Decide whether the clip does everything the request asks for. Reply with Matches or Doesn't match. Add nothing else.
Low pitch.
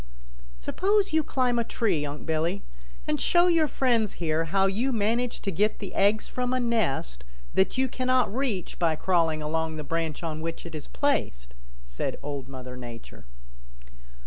Doesn't match